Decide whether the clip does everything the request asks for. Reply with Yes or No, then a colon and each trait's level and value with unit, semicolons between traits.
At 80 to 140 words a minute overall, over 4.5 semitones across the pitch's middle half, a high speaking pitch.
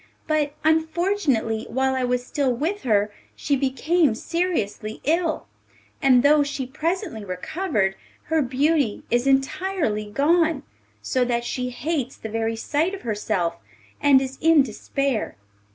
Yes: slow, 135 wpm; wide, 5.5 semitones; very high, 270 Hz